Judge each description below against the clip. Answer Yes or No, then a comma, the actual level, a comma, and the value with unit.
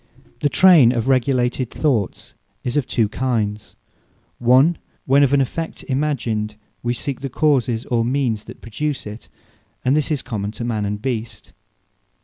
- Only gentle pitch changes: No, average, 3.7 semitones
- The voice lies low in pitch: Yes, low, 125 Hz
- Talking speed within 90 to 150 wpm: No, average, 160 wpm